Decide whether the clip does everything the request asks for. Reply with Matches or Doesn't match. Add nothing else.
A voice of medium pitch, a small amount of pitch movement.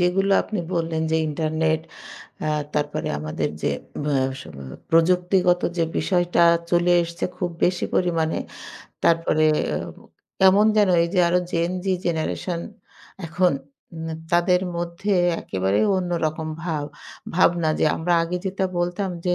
Matches